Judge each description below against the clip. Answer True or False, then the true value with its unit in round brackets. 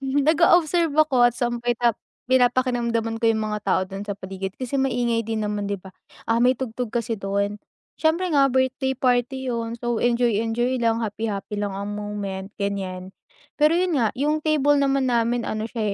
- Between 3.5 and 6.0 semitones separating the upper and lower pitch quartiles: True (4.2 semitones)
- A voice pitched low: False (235 Hz)